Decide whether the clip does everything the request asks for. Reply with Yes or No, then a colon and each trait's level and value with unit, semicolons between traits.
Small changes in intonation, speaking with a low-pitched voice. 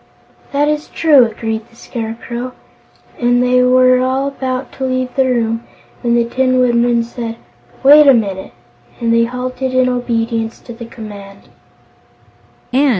No: narrow, 1.8 semitones; high, 245 Hz